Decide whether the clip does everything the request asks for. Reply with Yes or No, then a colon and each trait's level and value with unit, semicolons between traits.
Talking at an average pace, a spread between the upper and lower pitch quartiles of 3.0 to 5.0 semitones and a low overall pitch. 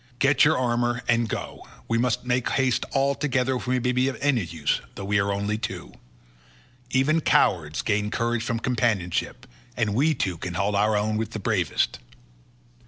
Yes: average, 180 wpm; average, 3.7 semitones; low, 115 Hz